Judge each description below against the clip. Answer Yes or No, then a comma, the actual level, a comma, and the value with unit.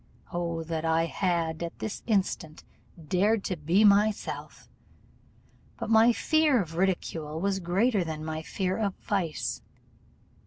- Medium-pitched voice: Yes, medium, 180 Hz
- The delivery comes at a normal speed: No, slow, 130 wpm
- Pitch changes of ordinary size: Yes, average, 3.9 semitones